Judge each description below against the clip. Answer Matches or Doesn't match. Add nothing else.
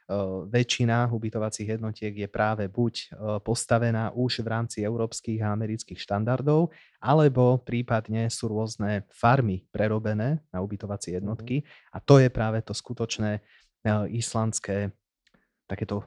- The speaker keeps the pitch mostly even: Matches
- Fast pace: Doesn't match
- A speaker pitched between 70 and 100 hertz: Doesn't match